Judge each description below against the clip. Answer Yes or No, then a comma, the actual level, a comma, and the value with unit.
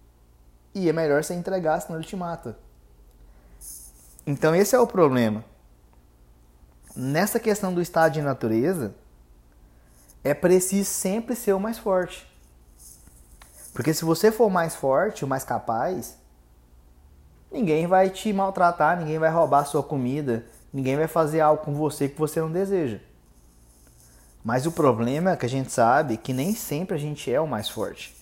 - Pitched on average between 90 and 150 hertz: Yes, low, 135 Hz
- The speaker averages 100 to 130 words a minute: No, average, 155 wpm